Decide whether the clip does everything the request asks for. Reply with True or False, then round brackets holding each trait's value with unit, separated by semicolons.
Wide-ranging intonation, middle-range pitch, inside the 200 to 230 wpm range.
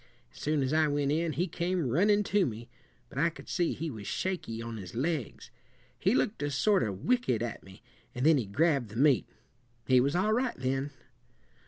True (6.3 semitones; 145 Hz; 205 wpm)